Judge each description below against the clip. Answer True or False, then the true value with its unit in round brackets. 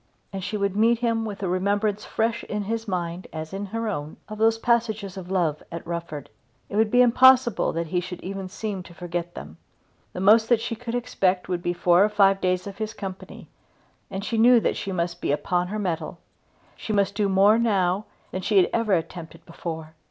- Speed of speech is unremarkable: False (210 wpm)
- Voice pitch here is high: True (195 Hz)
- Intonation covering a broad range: False (3.7 semitones)